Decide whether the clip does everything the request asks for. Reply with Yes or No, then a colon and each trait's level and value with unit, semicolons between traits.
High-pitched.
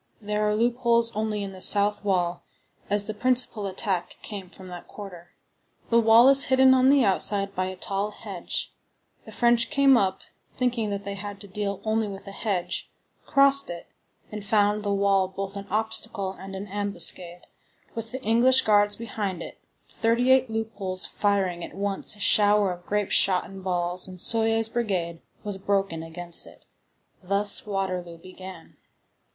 Yes: high, 205 Hz